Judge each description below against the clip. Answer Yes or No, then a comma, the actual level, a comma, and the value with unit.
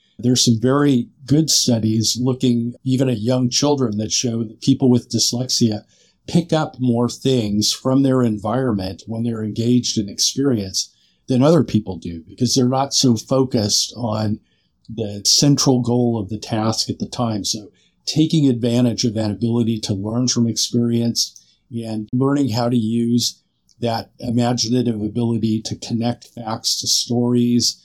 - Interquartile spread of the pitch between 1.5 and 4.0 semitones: Yes, narrow, 2.4 semitones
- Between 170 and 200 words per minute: No, average, 150 wpm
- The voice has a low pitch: Yes, low, 120 Hz